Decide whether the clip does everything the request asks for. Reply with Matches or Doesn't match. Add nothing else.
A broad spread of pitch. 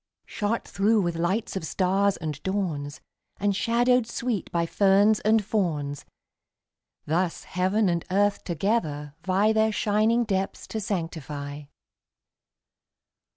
Doesn't match